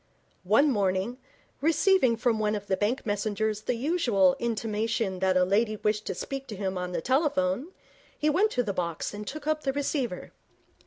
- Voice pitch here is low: No, high, 220 Hz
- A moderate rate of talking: Yes, average, 180 wpm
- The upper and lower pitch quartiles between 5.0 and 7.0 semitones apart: Yes, average, 5.3 semitones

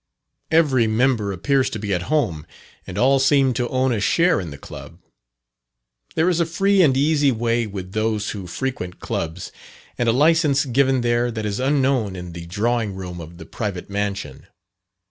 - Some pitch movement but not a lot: No, wide, 5.7 semitones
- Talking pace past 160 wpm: Yes, average, 180 wpm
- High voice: No, low, 120 Hz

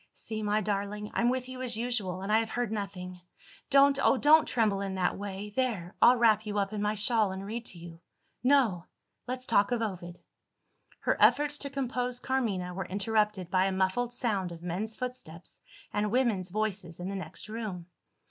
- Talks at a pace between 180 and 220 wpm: Yes, average, 190 wpm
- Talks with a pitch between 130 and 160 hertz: No, high, 210 Hz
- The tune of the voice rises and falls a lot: No, average, 4.4 semitones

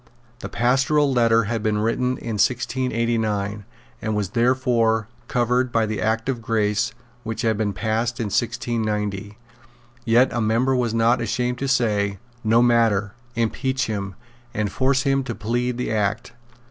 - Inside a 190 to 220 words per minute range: No, average, 150 wpm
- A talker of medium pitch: No, low, 115 Hz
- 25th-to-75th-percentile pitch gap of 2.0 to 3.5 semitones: Yes, narrow, 2.4 semitones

